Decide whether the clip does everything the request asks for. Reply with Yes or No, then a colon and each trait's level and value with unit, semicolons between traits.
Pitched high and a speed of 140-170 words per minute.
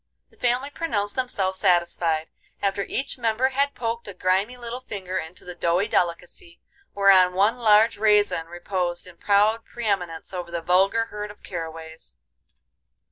Yes: high, 195 Hz; average, 150 wpm